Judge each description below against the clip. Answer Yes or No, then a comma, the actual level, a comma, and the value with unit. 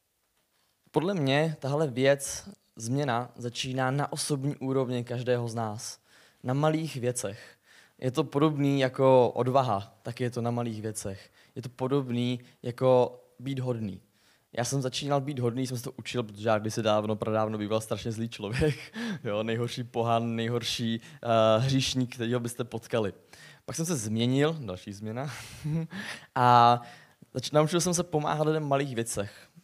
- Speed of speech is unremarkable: Yes, average, 150 wpm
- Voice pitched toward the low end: Yes, low, 125 Hz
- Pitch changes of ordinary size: Yes, average, 3.6 semitones